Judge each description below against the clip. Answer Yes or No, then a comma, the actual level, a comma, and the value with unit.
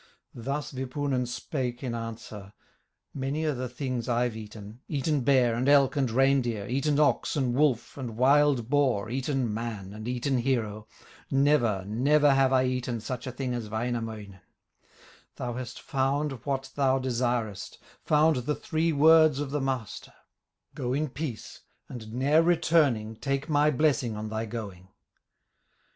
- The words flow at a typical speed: Yes, average, 150 wpm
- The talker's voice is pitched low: Yes, low, 130 Hz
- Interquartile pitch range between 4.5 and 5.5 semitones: No, average, 3.5 semitones